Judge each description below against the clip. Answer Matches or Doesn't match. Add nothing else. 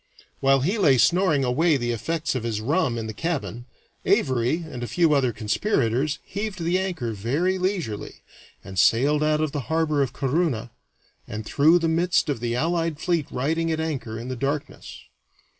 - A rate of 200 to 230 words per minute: Doesn't match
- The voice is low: Doesn't match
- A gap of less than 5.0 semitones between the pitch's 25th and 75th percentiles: Doesn't match